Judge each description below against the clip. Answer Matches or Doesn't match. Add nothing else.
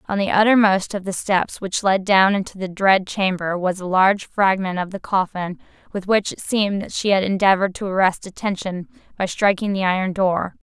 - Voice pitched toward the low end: Doesn't match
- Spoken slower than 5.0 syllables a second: Doesn't match